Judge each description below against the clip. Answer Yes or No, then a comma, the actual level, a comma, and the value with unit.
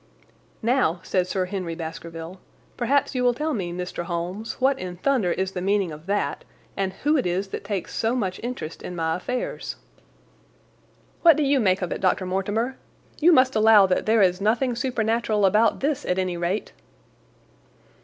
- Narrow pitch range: No, average, 5.2 semitones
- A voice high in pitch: Yes, high, 200 Hz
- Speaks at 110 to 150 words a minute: No, average, 175 wpm